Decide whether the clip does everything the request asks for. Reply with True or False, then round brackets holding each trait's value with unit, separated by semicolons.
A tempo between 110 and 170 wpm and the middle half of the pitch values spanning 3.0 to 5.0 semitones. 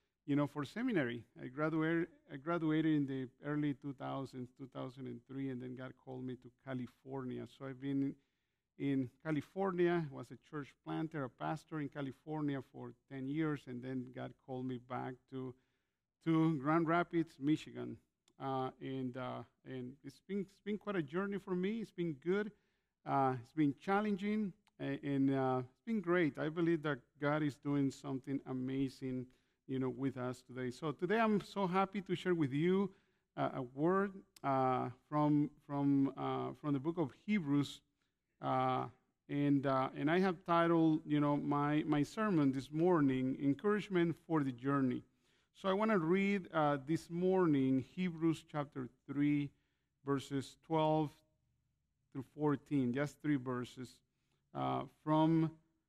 True (155 wpm; 3.9 semitones)